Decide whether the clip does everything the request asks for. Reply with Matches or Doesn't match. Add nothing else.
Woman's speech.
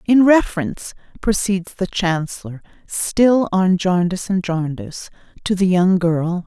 Matches